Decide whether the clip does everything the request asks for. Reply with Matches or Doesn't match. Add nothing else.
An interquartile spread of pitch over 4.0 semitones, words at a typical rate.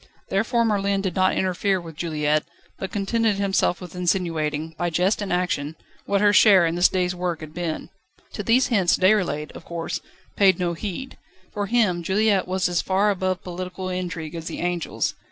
Doesn't match